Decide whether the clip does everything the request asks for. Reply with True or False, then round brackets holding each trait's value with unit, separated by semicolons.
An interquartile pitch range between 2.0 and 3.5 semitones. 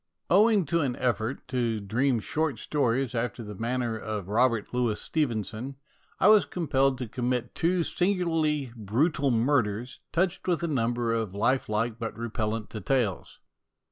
False (4.6 semitones)